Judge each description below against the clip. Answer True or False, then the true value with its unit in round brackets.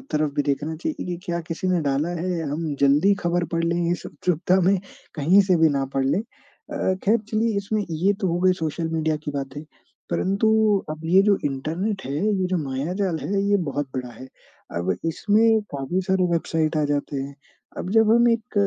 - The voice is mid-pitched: True (170 Hz)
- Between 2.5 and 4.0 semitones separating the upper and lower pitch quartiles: False (5.0 semitones)